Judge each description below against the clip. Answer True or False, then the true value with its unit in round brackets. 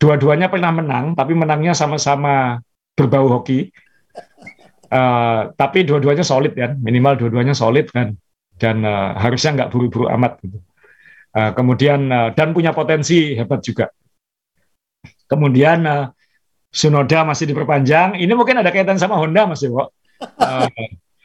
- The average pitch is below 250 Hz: True (140 Hz)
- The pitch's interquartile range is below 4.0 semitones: False (4.3 semitones)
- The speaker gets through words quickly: False (130 wpm)